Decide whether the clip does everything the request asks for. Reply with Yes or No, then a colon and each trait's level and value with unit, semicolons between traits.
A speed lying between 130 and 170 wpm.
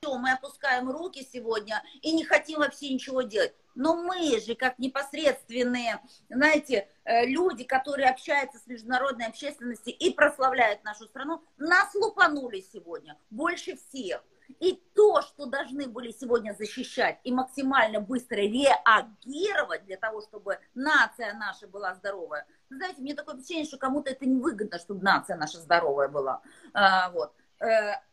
Yes: average, 135 wpm